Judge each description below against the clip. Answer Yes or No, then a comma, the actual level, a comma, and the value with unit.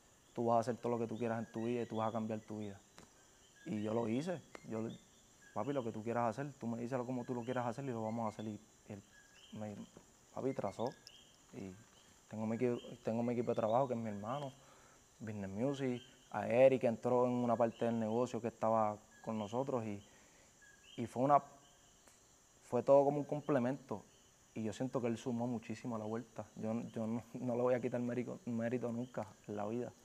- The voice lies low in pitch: Yes, low, 120 Hz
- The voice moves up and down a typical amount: No, narrow, 2.3 semitones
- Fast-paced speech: Yes, fast, 220 wpm